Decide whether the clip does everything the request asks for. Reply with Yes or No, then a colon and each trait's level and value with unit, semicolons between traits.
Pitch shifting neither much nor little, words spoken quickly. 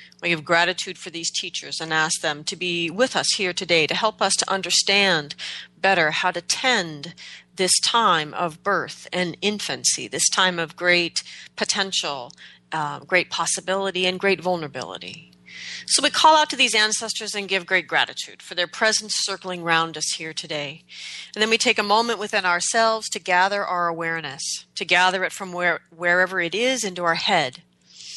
No: average, 3.1 semitones; average, 175 wpm